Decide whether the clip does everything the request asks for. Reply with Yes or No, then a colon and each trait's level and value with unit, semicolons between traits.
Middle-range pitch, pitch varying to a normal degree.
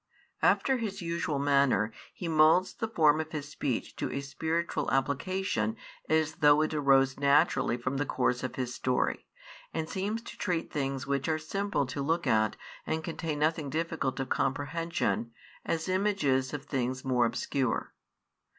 Yes: medium, 145 Hz; average, 3.6 semitones